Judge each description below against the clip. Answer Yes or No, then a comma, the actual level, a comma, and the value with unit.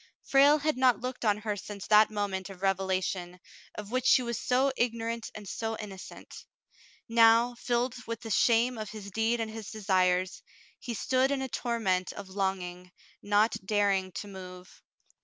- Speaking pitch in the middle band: No, high, 215 Hz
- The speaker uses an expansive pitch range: No, average, 3.6 semitones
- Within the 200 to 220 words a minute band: No, average, 170 wpm